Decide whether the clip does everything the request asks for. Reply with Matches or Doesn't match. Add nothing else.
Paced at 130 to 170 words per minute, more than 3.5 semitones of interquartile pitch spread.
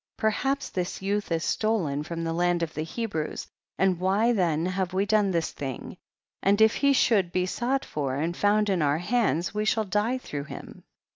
Doesn't match